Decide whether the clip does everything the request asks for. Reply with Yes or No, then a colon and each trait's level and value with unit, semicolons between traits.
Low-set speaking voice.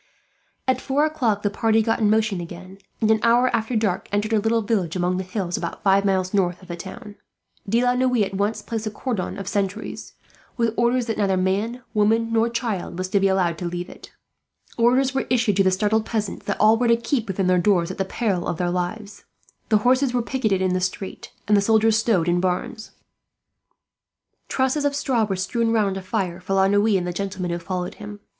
No: high, 205 Hz